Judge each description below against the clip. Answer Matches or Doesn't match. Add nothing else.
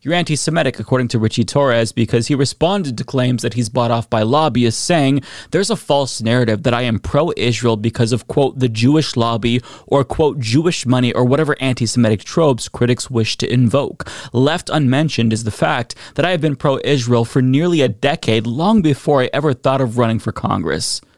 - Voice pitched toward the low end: Matches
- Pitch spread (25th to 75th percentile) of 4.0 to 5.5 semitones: Doesn't match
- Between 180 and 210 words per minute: Matches